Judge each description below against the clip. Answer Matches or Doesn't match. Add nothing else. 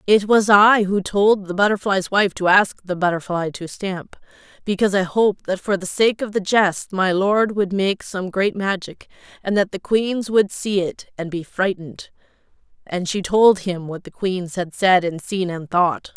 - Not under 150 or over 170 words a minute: Doesn't match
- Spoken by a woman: Matches